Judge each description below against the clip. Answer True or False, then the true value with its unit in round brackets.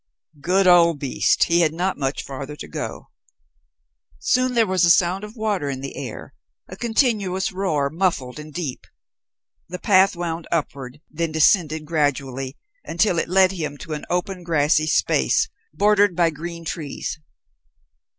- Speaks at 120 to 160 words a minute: True (150 wpm)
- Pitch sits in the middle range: True (170 Hz)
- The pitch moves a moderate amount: True (4.1 semitones)